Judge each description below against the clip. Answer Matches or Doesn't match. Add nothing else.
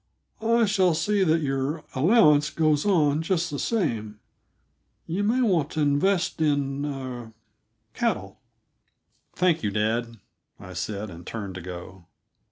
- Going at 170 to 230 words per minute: Doesn't match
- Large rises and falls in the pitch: Matches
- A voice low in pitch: Doesn't match